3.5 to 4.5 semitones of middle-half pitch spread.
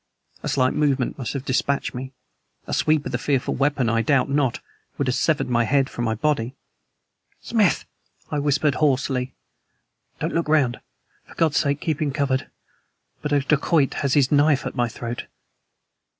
No: narrow, 2.6 semitones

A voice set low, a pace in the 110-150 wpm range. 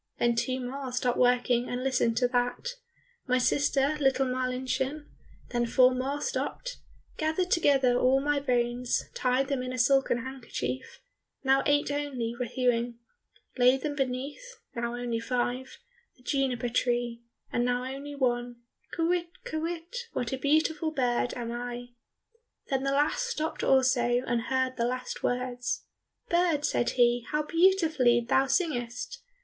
No: very high, 255 Hz; average, 145 wpm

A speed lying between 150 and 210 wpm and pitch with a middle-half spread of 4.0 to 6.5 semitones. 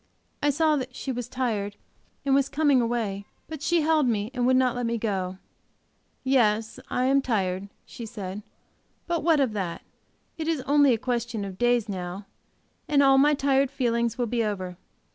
Yes: average, 180 wpm; average, 4.6 semitones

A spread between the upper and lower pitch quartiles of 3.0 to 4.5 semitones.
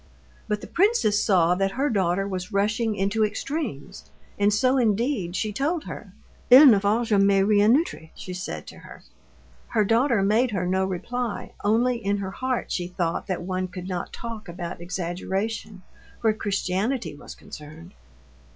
Yes: average, 3.8 semitones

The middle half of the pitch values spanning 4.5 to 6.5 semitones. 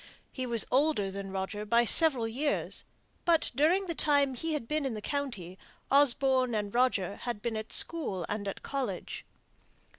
Yes: wide, 5.5 semitones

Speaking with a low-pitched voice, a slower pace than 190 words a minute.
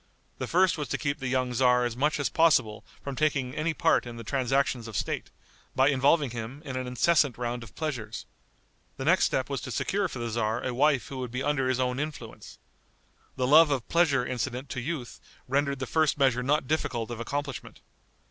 No: low, 130 Hz; fast, 205 wpm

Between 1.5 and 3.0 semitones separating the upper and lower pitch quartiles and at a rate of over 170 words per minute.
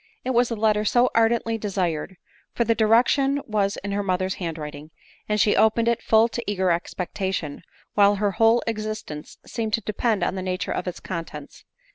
No: average, 3.6 semitones; average, 190 wpm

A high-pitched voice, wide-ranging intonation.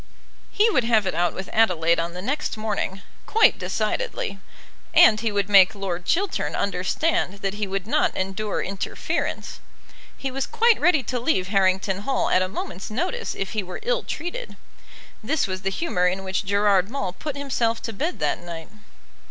Yes: high, 205 Hz; wide, 6.5 semitones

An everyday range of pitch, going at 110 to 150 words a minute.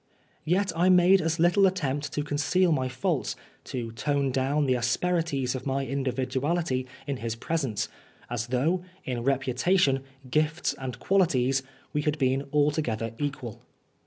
Yes: average, 4.1 semitones; average, 145 wpm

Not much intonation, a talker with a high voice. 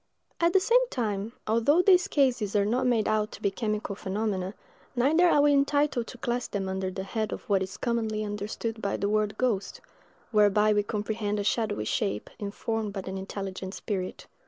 No: average, 3.2 semitones; high, 215 Hz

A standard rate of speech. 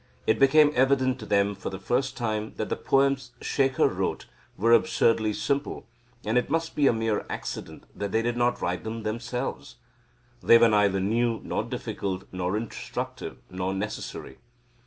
Yes: average, 165 wpm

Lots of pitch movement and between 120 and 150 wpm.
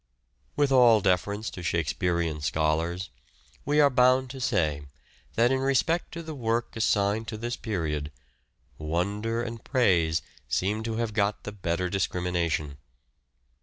Yes: wide, 5.8 semitones; average, 140 wpm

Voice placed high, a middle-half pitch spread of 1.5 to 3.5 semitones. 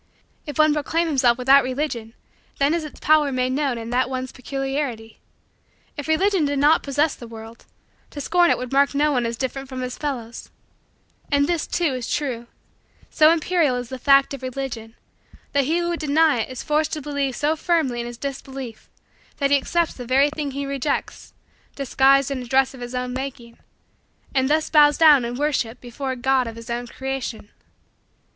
Yes: very high, 270 Hz; average, 3.0 semitones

